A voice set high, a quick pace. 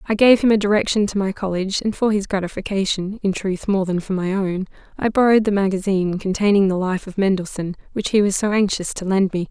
Yes: high, 195 Hz; fast, 225 wpm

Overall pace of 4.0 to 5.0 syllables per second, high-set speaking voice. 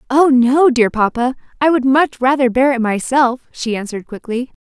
Yes: 4.9 syllables/s; very high, 255 Hz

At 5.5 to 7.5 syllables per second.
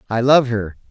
No: 5.0 syllables/s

